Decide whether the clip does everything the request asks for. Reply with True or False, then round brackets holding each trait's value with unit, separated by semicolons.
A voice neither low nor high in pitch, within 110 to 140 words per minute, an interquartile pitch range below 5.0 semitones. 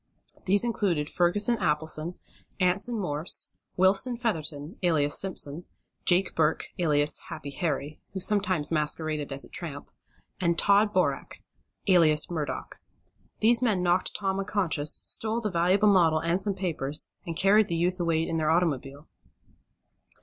True (175 Hz; 135 wpm; 4.1 semitones)